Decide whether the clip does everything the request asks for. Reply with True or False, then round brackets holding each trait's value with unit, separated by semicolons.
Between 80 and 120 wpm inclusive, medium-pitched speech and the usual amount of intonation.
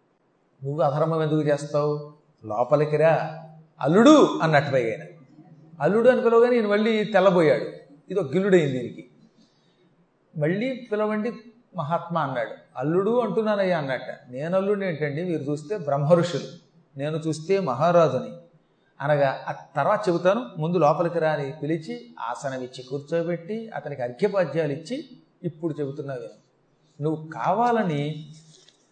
True (100 wpm; 160 Hz; 4.4 semitones)